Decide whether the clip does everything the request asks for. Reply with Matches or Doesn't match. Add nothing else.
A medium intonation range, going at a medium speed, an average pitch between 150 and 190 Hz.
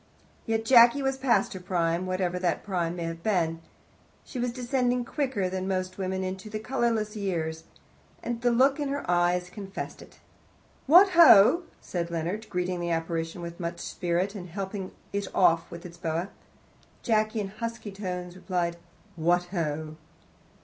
Matches